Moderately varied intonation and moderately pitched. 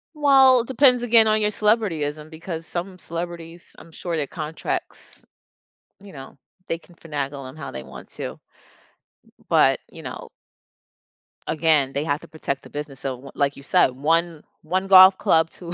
Yes: average, 4.5 semitones; medium, 165 Hz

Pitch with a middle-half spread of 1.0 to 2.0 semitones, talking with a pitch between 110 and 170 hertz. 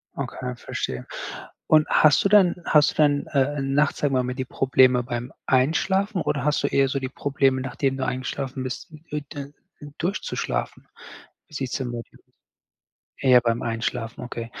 No: narrow, 2.5 semitones; low, 135 Hz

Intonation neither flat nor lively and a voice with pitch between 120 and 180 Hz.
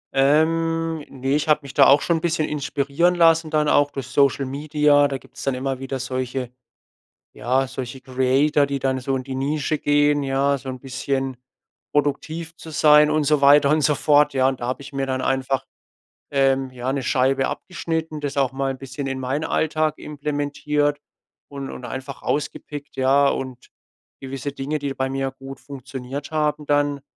No: narrow, 1.9 semitones; medium, 140 Hz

